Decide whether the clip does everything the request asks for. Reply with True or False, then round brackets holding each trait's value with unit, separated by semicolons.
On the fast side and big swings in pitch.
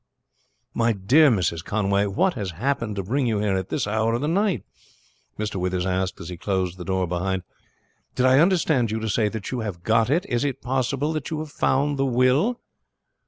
True (210 wpm; 6.2 semitones)